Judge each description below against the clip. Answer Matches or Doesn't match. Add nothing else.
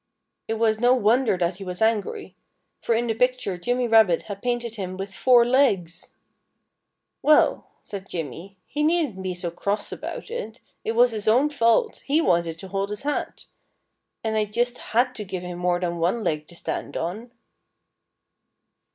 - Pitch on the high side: Matches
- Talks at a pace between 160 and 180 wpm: Matches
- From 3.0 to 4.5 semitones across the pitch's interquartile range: Doesn't match